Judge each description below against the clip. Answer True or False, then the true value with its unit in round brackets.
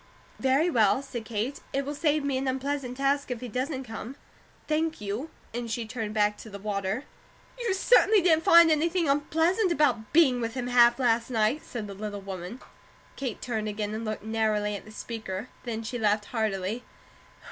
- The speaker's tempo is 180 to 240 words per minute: True (185 wpm)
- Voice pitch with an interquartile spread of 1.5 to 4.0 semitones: False (4.7 semitones)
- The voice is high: True (240 Hz)